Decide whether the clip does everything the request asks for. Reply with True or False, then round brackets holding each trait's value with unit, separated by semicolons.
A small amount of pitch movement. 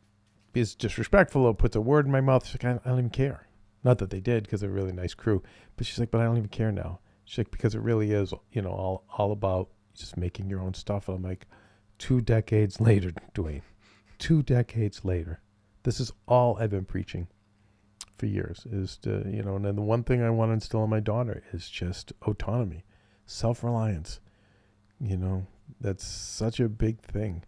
False (3.0 semitones)